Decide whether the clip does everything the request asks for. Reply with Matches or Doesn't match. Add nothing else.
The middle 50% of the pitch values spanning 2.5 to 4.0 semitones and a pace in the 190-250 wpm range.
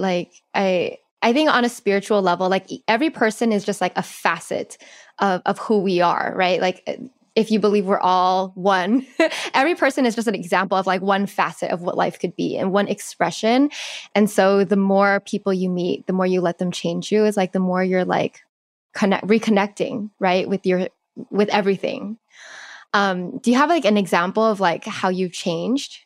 Matches